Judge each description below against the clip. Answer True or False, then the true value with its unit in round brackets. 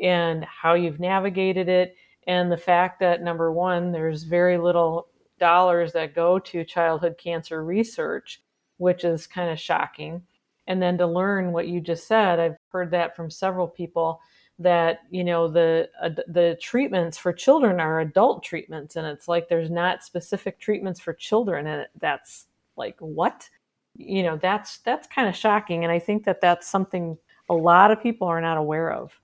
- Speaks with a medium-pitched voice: True (175 Hz)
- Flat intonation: True (1.8 semitones)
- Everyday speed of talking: True (175 wpm)